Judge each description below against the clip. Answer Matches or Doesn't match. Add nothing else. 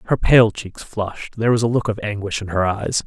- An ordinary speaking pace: Doesn't match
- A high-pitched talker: Doesn't match